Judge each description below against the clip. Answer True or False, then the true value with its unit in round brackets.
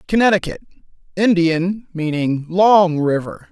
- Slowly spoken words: True (70 wpm)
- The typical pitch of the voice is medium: True (175 Hz)